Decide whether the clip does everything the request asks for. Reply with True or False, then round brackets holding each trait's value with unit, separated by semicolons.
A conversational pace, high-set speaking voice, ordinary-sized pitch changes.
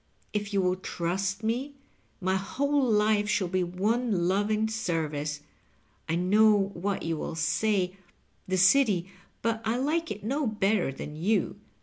True (150 wpm; 200 Hz; 3.3 semitones)